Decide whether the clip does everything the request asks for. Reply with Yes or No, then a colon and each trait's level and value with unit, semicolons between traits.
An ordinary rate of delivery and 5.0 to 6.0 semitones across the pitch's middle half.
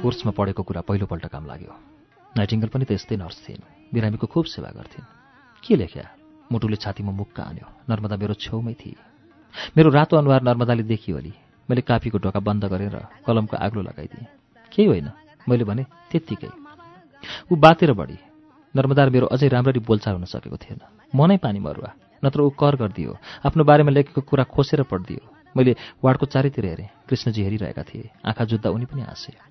Yes: average, 165 wpm; wide, 5.4 semitones